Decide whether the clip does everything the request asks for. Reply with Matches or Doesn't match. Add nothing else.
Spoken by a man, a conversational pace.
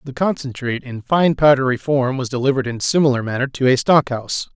Matches